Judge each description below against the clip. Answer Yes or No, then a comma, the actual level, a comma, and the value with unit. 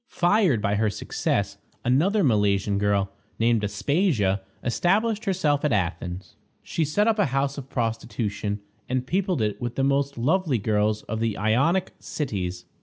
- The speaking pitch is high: No, low, 120 Hz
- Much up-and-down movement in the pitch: Yes, wide, 7.3 semitones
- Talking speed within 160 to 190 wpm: No, average, 150 wpm